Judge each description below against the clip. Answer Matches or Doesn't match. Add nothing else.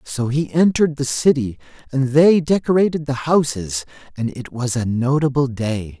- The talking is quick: Doesn't match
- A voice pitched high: Doesn't match